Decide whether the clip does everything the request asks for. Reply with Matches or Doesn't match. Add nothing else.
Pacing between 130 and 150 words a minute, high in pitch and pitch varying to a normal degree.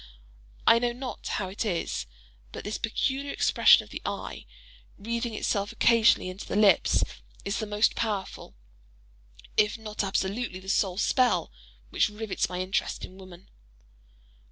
Matches